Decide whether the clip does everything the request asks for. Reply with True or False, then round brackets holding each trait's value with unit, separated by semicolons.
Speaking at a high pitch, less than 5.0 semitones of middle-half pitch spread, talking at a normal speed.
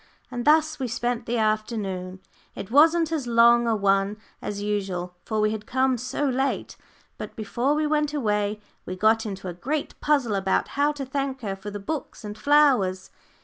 False (230 Hz; 5.3 semitones; 185 wpm)